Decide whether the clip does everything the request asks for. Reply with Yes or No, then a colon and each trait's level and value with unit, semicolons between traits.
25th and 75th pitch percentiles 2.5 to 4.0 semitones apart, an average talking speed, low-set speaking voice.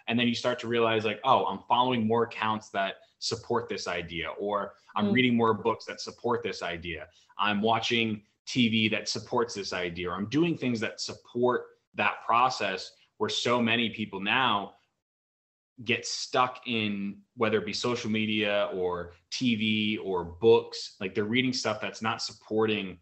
Yes: average, 3.1 semitones; average, 165 wpm; low, 110 Hz